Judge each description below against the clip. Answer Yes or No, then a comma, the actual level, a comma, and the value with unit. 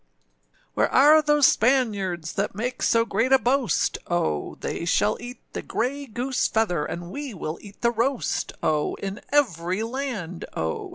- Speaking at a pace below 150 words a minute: No, average, 160 wpm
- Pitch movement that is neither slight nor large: No, wide, 6.8 semitones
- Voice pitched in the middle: No, high, 225 Hz